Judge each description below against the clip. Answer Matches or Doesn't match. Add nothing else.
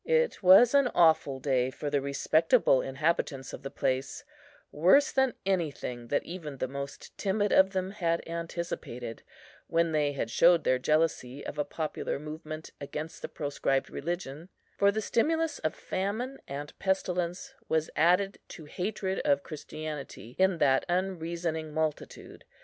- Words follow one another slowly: Doesn't match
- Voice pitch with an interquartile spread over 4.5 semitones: Matches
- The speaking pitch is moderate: Matches